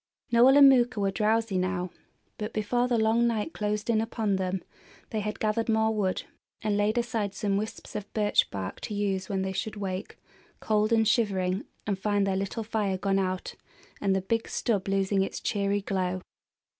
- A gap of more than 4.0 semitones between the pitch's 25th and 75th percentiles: No, narrow, 2.4 semitones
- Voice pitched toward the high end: Yes, high, 205 Hz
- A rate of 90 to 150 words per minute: No, average, 185 wpm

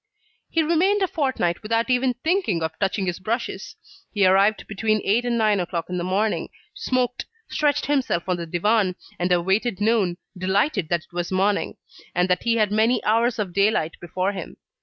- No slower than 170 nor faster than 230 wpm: Yes, average, 180 wpm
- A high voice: Yes, high, 205 Hz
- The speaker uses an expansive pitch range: No, average, 4.6 semitones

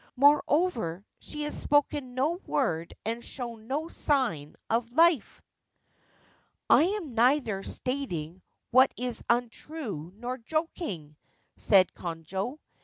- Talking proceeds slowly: Yes, slow, 110 wpm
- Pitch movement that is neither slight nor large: No, wide, 6.9 semitones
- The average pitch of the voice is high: Yes, high, 245 Hz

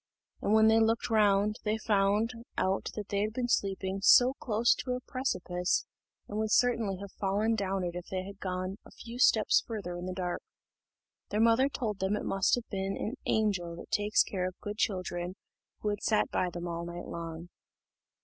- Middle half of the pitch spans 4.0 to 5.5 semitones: No, average, 3.0 semitones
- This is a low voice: No, high, 200 Hz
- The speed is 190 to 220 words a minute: Yes, average, 195 wpm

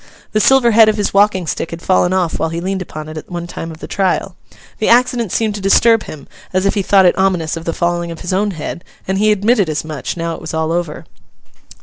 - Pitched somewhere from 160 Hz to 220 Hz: Yes, medium, 185 Hz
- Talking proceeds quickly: Yes, fast, 255 wpm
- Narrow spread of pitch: No, average, 3.8 semitones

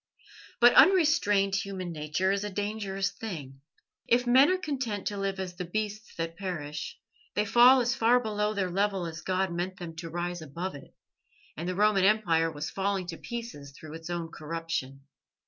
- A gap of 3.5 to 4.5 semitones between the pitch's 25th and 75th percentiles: Yes, average, 4.2 semitones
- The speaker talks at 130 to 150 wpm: No, average, 180 wpm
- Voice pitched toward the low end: No, high, 190 Hz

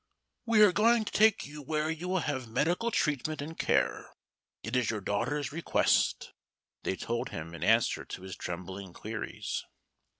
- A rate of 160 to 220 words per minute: Yes, average, 165 wpm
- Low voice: No, medium, 145 Hz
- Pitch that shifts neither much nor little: No, wide, 8.2 semitones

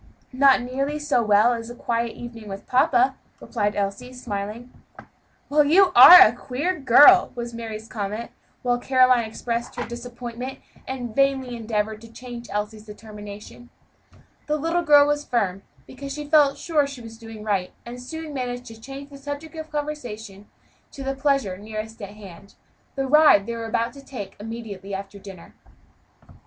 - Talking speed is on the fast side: No, average, 160 wpm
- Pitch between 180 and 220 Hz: No, high, 240 Hz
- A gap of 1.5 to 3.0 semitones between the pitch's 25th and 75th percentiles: No, average, 4.2 semitones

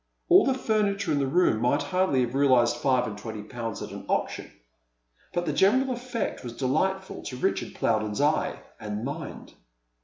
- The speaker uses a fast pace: No, average, 175 wpm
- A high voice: No, medium, 140 Hz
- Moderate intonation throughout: No, wide, 8.0 semitones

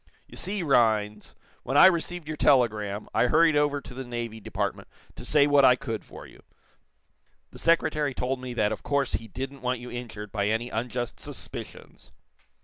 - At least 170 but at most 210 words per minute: Yes, average, 180 wpm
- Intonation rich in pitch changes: No, average, 4.4 semitones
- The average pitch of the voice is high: No, low, 125 Hz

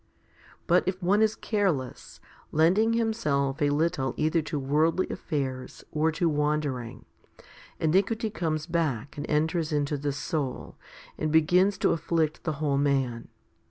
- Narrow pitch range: No, average, 3.6 semitones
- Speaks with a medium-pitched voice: Yes, medium, 155 Hz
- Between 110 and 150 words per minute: Yes, slow, 135 wpm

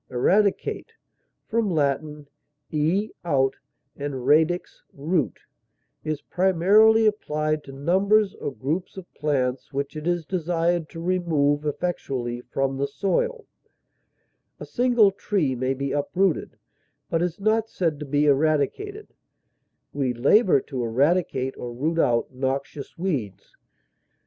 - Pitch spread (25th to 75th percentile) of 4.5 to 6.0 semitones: Yes, average, 5.1 semitones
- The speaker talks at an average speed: No, slow, 120 wpm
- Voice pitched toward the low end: No, medium, 155 Hz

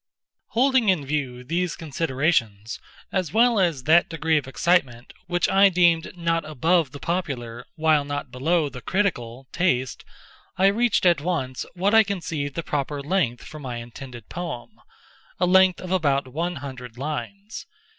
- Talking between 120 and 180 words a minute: Yes, average, 150 wpm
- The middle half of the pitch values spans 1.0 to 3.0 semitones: No, wide, 5.4 semitones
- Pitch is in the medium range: Yes, medium, 160 Hz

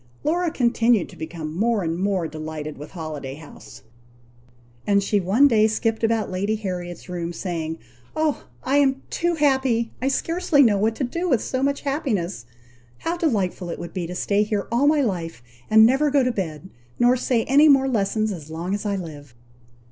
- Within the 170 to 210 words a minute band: Yes, average, 190 wpm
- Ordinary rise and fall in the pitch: No, wide, 7.3 semitones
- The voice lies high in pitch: Yes, high, 215 Hz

